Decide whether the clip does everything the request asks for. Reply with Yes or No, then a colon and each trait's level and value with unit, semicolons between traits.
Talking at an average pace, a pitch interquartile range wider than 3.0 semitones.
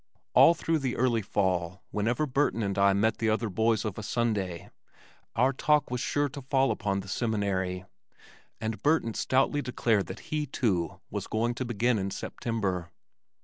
Yes: average, 170 wpm; average, 4.5 semitones